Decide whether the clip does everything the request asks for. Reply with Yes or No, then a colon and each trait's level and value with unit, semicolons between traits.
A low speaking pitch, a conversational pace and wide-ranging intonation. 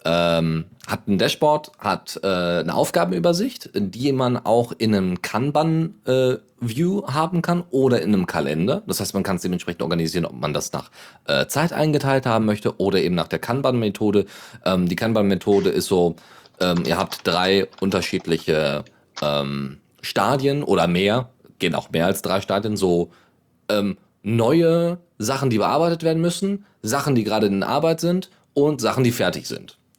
Yes: low, 115 Hz; average, 165 wpm; wide, 8.0 semitones